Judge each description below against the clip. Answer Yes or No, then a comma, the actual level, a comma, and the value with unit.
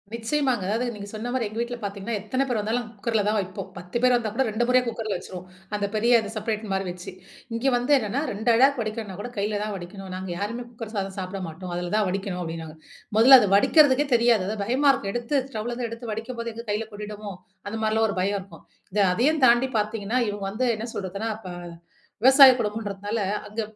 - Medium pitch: No, high, 215 Hz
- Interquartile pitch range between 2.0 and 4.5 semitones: Yes, average, 3.1 semitones